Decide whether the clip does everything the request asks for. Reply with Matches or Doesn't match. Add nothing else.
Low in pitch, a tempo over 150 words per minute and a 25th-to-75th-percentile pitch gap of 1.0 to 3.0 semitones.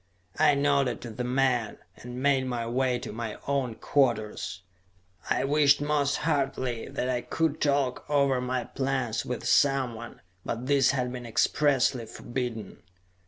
Doesn't match